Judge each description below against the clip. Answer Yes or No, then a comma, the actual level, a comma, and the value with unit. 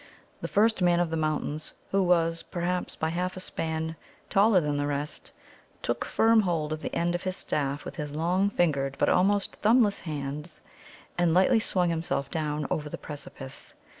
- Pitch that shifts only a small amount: No, average, 3.5 semitones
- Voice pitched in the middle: Yes, medium, 165 Hz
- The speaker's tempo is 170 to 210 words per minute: Yes, average, 180 wpm